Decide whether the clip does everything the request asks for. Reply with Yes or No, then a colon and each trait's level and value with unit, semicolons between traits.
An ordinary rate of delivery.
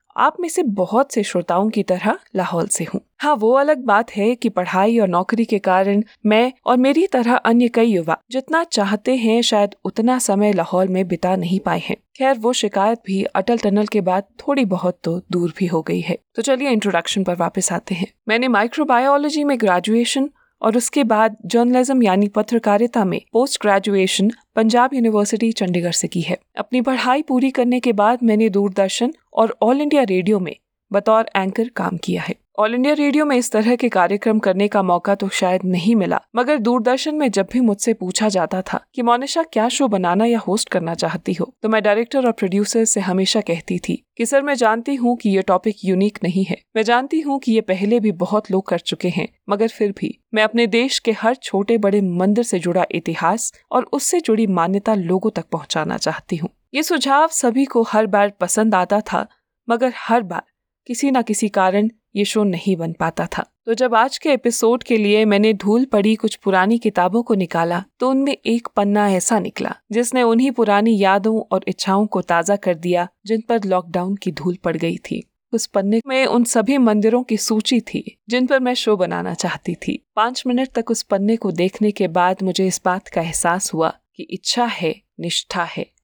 No: fast, 200 wpm